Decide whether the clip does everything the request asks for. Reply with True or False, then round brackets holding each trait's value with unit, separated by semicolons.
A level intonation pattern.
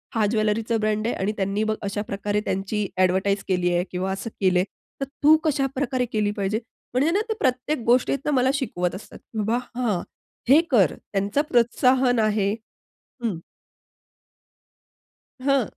False (4.3 semitones)